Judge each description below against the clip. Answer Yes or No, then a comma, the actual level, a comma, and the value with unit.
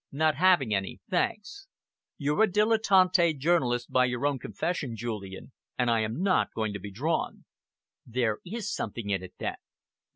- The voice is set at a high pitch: No, low, 135 Hz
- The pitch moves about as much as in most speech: No, wide, 8.4 semitones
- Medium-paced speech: Yes, average, 160 wpm